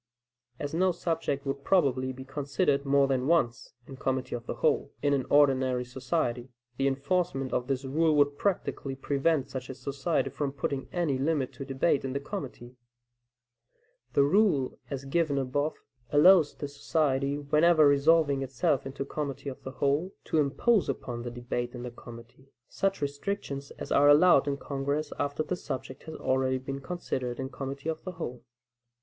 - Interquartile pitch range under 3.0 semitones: Yes, narrow, 2.6 semitones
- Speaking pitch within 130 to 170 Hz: Yes, medium, 140 Hz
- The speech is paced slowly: No, average, 170 wpm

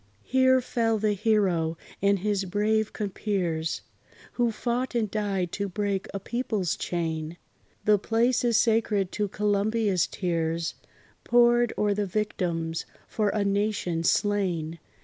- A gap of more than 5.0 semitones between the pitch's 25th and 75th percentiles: No, average, 3.5 semitones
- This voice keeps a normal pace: No, slow, 130 wpm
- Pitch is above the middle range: Yes, high, 205 Hz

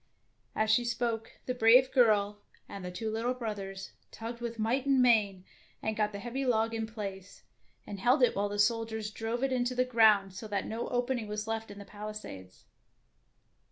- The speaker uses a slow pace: No, average, 190 wpm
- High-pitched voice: Yes, high, 225 Hz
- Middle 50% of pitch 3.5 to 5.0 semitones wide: No, average, 2.7 semitones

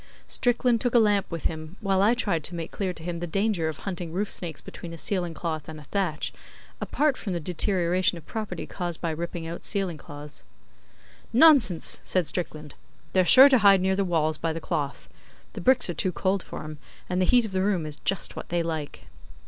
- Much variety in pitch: No, average, 3.6 semitones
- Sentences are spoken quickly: Yes, fast, 215 wpm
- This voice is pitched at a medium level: Yes, medium, 180 Hz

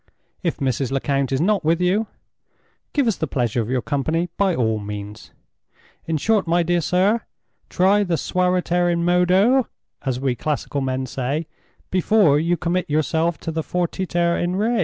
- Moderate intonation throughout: Yes, average, 4.8 semitones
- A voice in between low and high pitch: Yes, medium, 170 Hz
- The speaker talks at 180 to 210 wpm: No, average, 165 wpm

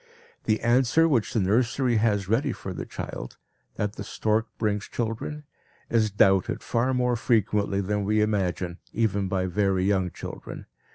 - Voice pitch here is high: No, low, 105 Hz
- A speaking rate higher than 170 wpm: No, average, 155 wpm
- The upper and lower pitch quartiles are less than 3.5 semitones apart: Yes, average, 3.1 semitones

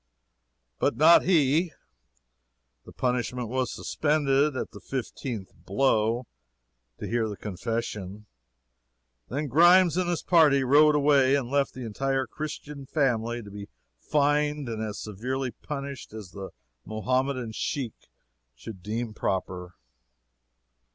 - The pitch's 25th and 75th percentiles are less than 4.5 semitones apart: No, average, 4.8 semitones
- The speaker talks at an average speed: No, slow, 120 wpm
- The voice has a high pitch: No, low, 130 Hz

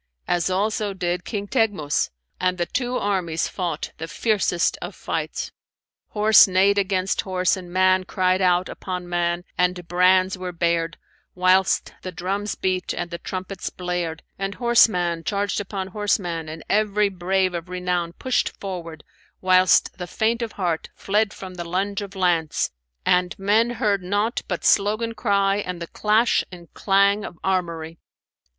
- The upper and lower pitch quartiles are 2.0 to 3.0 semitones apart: Yes, narrow, 2.4 semitones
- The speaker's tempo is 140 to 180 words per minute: Yes, average, 155 wpm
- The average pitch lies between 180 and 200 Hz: Yes, medium, 185 Hz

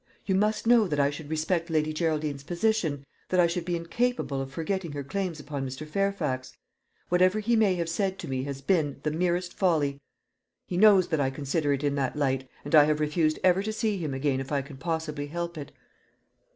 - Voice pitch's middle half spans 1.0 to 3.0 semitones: No, average, 4.4 semitones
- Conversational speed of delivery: No, fast, 210 wpm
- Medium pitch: Yes, medium, 160 Hz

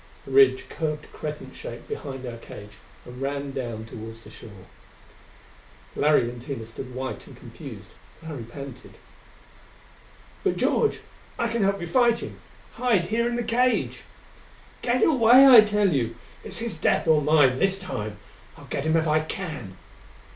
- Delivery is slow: No, average, 160 wpm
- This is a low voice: No, medium, 150 Hz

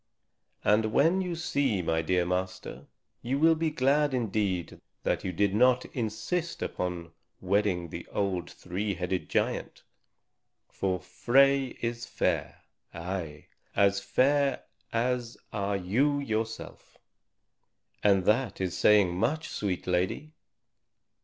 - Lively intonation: Yes, wide, 6.3 semitones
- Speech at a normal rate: No, slow, 120 wpm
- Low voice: Yes, low, 105 Hz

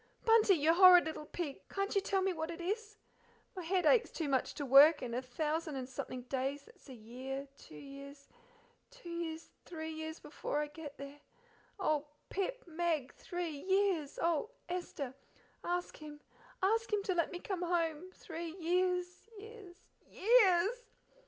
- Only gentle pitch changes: No, average, 4.3 semitones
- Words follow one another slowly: No, average, 165 wpm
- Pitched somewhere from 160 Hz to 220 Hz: No, very high, 335 Hz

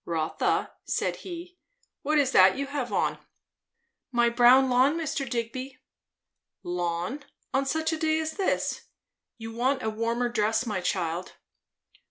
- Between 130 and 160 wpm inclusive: Yes, average, 140 wpm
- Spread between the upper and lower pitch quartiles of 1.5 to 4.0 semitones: No, average, 4.4 semitones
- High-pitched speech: Yes, high, 245 Hz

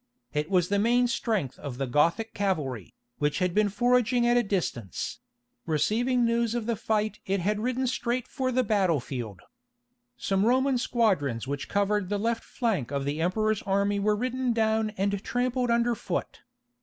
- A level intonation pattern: No, average, 5.1 semitones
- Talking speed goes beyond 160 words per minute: Yes, average, 170 wpm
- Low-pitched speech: No, high, 210 Hz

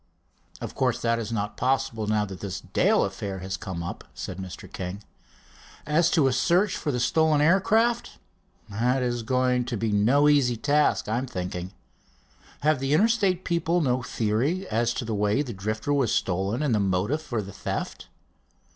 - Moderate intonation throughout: No, wide, 6.1 semitones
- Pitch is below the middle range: Yes, low, 120 Hz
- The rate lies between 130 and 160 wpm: No, average, 175 wpm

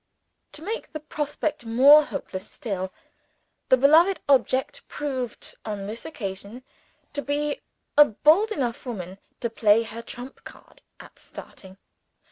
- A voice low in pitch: No, very high, 260 Hz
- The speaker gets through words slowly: Yes, slow, 130 wpm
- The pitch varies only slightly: No, average, 5.3 semitones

